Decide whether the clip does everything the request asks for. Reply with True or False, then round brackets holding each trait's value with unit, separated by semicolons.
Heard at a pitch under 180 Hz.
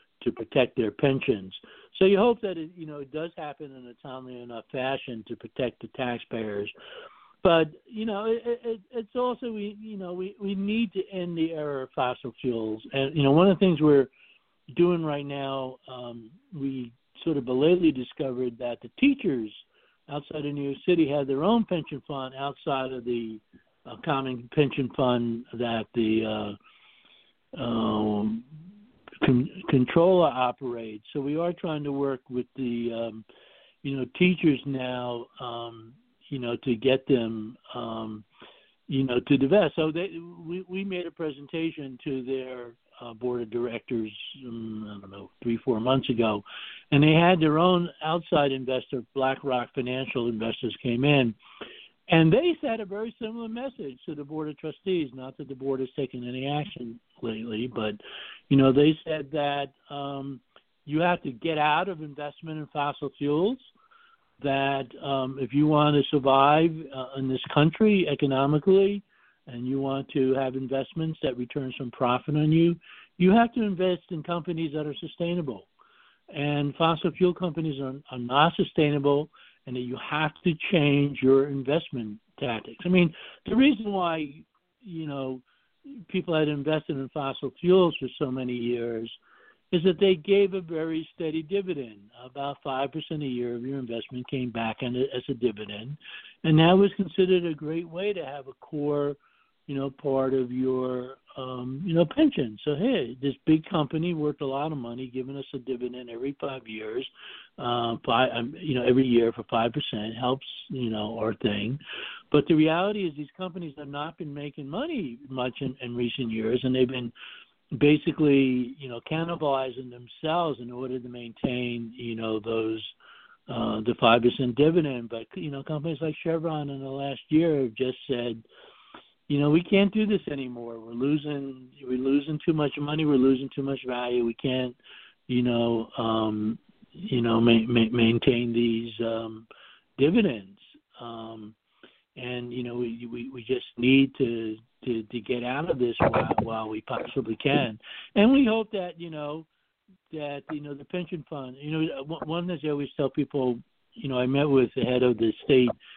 True (140 Hz)